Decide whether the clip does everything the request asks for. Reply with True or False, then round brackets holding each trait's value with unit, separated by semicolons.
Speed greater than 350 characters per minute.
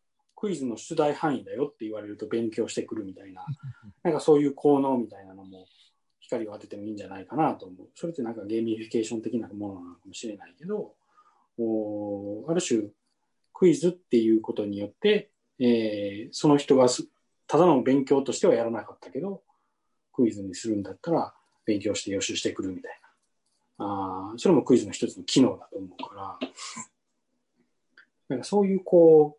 True (380 characters per minute)